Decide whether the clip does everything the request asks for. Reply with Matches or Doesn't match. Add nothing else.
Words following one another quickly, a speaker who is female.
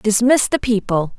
Doesn't match